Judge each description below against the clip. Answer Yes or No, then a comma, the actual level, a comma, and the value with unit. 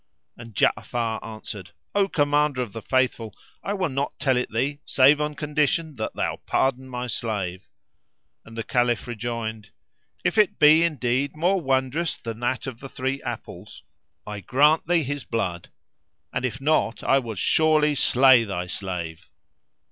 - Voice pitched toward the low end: Yes, low, 130 Hz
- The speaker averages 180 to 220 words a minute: No, average, 155 wpm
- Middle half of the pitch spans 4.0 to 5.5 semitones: Yes, average, 4.6 semitones